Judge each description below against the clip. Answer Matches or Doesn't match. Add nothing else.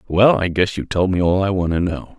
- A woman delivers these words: Doesn't match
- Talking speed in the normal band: Doesn't match